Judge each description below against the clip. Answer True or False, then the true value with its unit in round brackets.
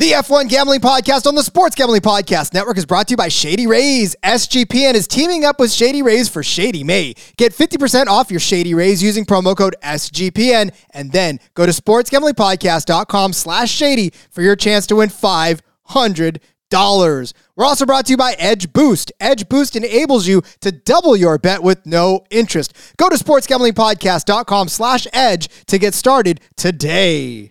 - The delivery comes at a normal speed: True (170 wpm)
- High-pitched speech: True (210 Hz)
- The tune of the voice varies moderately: False (6.1 semitones)